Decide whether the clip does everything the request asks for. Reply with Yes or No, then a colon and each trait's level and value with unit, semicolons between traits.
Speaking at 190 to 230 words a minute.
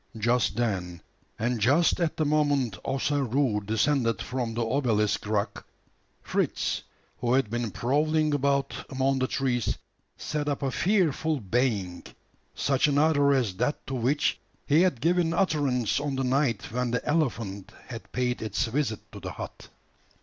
No: average, 150 wpm